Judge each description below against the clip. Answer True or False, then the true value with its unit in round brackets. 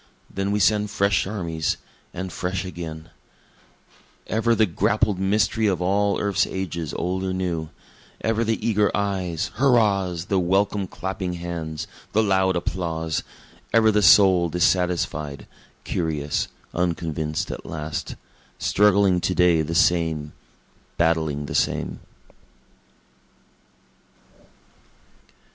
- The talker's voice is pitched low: True (90 Hz)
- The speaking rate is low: True (110 wpm)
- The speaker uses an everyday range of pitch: True (3.5 semitones)